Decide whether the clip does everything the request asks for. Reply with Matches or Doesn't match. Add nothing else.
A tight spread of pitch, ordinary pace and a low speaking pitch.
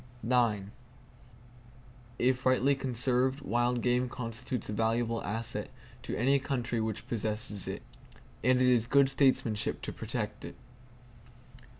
Doesn't match